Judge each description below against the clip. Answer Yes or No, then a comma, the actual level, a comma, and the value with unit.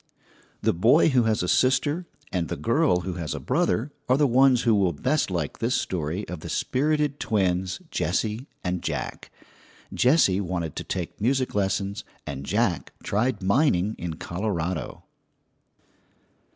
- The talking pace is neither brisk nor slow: Yes, average, 150 wpm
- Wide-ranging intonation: Yes, wide, 6.4 semitones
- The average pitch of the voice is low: Yes, low, 100 Hz